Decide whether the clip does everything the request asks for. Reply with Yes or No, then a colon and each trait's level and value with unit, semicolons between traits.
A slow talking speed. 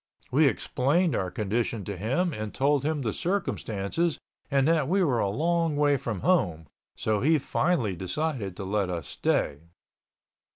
No: average, 160 wpm